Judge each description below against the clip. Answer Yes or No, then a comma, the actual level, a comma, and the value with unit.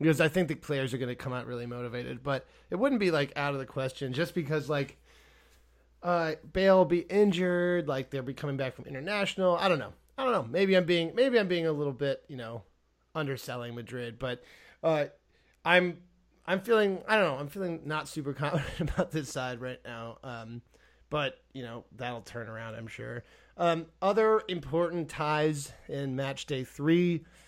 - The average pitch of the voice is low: No, medium, 150 Hz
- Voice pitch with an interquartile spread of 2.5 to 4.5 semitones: No, wide, 5.5 semitones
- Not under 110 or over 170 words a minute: No, average, 190 wpm